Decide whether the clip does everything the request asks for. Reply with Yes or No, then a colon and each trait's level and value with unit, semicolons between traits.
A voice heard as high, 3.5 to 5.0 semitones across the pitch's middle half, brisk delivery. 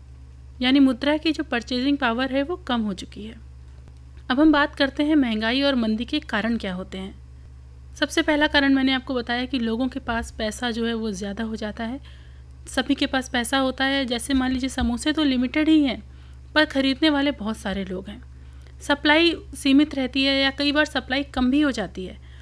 No: very high, 255 Hz; wide, 5.5 semitones; fast, 205 wpm